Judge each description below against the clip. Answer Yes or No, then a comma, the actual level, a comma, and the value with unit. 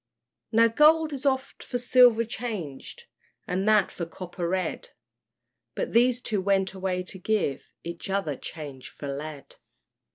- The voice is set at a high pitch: Yes, high, 195 Hz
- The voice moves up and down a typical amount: No, wide, 5.9 semitones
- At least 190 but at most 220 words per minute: No, average, 140 wpm